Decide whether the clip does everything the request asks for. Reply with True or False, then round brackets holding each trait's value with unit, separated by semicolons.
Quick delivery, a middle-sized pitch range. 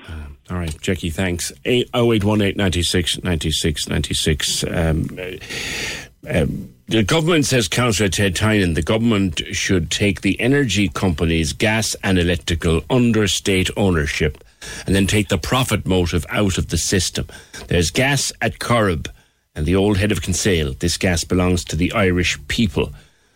False (135 wpm; 3.6 semitones)